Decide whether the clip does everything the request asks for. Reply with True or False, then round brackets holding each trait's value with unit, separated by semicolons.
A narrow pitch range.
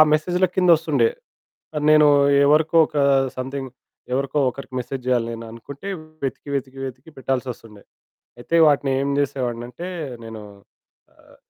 False (3.4 semitones)